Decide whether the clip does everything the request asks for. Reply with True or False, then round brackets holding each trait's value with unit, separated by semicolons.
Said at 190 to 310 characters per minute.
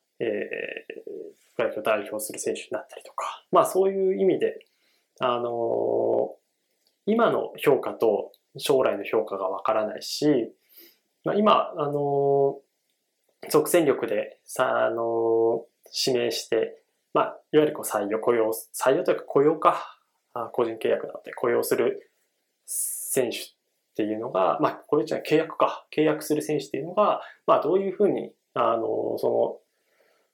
True (280 characters per minute)